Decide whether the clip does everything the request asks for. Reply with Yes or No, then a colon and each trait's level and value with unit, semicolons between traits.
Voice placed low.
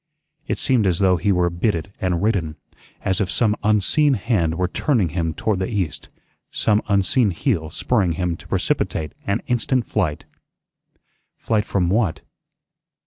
Yes: very low, 95 Hz